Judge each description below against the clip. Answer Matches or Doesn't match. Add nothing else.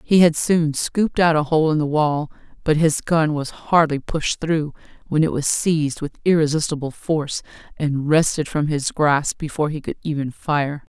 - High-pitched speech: Doesn't match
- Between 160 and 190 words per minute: Matches